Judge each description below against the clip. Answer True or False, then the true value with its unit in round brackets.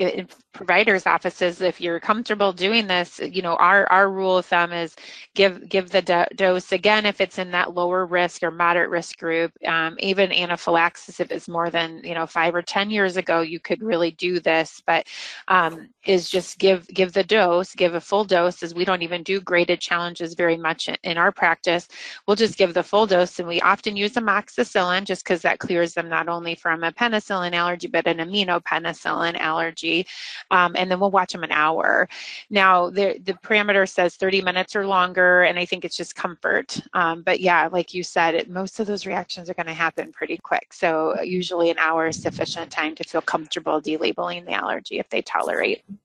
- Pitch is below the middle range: False (175 Hz)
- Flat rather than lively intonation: True (2.2 semitones)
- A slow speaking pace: False (205 wpm)